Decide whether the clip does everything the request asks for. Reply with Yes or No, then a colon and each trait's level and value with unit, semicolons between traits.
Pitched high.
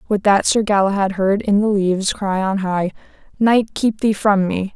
Yes: high, 200 Hz